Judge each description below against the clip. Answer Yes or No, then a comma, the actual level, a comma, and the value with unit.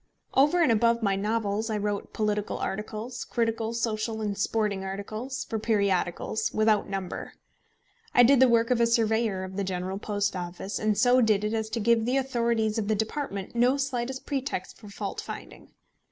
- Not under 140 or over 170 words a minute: No, average, 180 wpm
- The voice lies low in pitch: No, high, 220 Hz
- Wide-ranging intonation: No, narrow, 2.5 semitones